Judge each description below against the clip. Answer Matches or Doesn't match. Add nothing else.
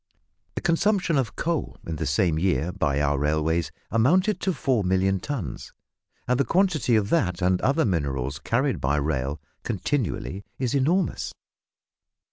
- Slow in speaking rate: Doesn't match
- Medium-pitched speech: Doesn't match